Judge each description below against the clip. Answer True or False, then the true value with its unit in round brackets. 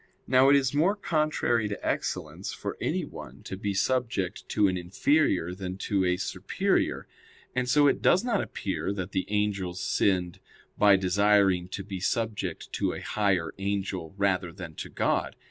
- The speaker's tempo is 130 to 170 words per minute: True (165 wpm)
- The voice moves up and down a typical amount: True (4.6 semitones)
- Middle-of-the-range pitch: False (100 Hz)